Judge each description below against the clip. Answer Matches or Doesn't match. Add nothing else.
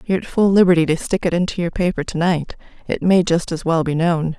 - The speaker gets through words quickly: Matches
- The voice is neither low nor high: Matches